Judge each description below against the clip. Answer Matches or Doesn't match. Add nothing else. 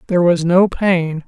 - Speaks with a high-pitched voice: Doesn't match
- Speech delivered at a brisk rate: Doesn't match